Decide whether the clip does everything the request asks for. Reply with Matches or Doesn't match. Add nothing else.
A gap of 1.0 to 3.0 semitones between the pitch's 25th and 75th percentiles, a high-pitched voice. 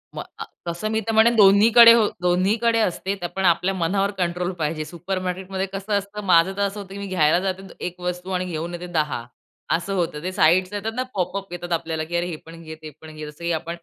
Doesn't match